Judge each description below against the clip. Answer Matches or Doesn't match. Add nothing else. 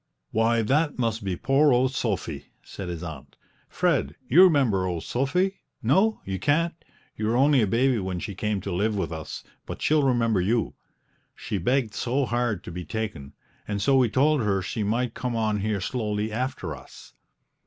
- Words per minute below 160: Doesn't match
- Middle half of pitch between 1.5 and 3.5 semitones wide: Doesn't match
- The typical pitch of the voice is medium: Doesn't match